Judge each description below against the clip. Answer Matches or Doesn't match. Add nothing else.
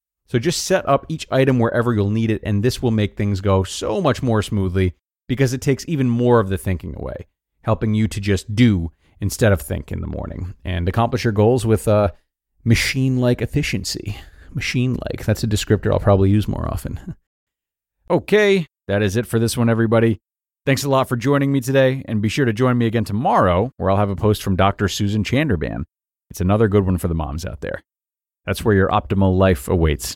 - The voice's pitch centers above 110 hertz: Doesn't match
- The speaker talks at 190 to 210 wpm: Matches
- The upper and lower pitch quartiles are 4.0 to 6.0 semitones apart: Matches